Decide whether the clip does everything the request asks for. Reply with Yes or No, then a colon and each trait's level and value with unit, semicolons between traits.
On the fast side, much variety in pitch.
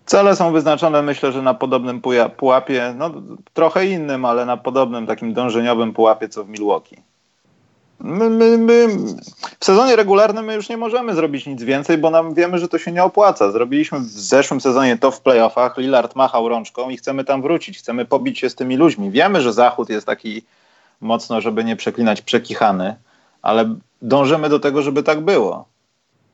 Yes: fast, 180 wpm; wide, 5.9 semitones